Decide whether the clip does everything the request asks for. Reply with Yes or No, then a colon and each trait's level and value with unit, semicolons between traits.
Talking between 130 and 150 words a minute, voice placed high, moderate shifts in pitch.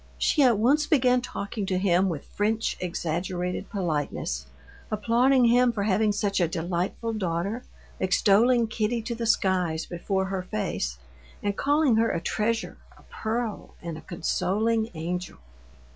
Yes: average, 145 wpm; high, 205 Hz; average, 4.4 semitones